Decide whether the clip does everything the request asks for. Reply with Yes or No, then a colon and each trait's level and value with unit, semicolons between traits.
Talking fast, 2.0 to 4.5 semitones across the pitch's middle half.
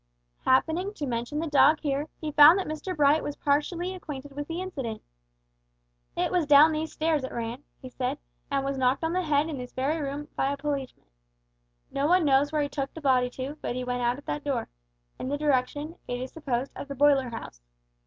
Yes: fast, 215 wpm; average, 2.9 semitones